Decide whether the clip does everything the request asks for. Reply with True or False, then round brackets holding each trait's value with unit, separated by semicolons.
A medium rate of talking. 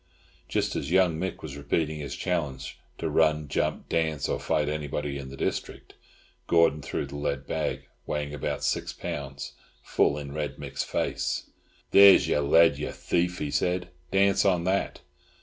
True (165 wpm)